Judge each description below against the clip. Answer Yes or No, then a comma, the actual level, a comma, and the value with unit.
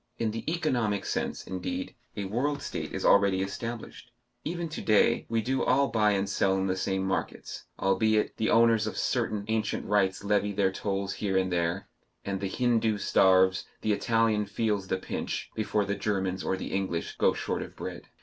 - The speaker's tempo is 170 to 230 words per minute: Yes, average, 185 wpm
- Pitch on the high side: No, low, 105 Hz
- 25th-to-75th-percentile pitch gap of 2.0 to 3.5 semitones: Yes, average, 2.9 semitones